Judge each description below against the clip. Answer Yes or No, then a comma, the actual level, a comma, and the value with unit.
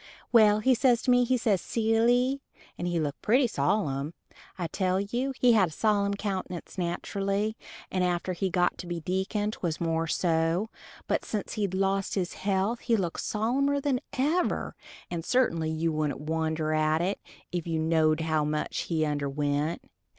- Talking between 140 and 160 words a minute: No, average, 170 wpm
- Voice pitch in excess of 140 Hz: Yes, medium, 185 Hz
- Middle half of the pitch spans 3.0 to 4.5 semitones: No, average, 5.1 semitones